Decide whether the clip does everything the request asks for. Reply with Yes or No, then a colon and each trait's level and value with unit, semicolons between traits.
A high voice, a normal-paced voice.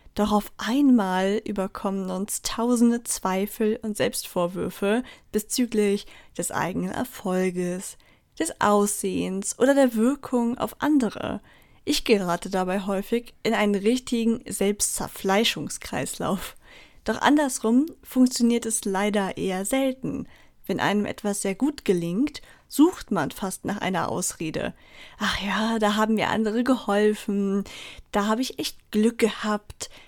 No: high, 215 Hz; slow, 120 wpm